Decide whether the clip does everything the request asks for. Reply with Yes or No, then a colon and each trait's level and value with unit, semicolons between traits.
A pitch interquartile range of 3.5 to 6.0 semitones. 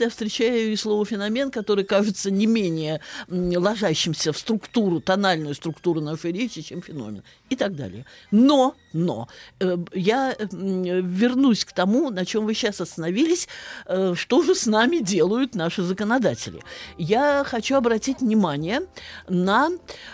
Yes: average, 5.2 semitones